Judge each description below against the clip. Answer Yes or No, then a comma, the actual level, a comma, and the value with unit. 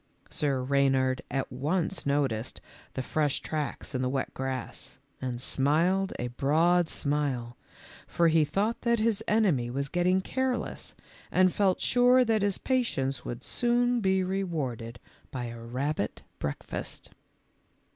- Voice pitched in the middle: Yes, medium, 150 Hz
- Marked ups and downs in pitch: Yes, wide, 6.7 semitones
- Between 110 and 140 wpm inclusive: Yes, slow, 135 wpm